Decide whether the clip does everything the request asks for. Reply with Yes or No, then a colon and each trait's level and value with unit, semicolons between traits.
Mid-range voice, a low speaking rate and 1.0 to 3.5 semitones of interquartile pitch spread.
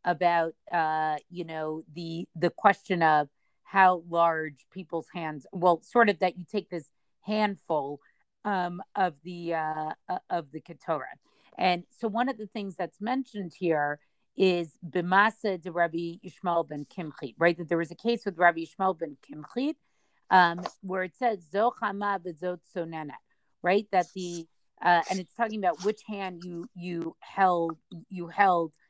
No: medium, 175 Hz; average, 150 wpm; average, 2.7 semitones